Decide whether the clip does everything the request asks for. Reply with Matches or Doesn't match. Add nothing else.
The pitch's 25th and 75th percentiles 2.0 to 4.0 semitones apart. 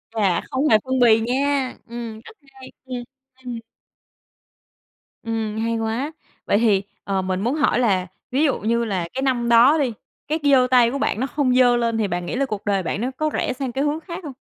Matches